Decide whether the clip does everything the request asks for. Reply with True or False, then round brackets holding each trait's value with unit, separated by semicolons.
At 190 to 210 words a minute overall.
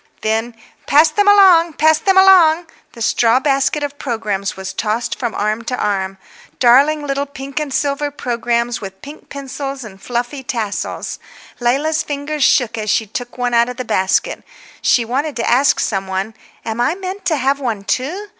False (175 wpm)